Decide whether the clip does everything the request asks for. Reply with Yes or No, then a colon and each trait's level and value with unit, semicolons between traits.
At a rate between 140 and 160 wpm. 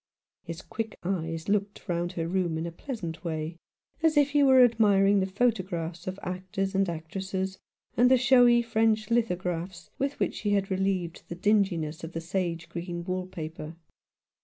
No: average, 170 wpm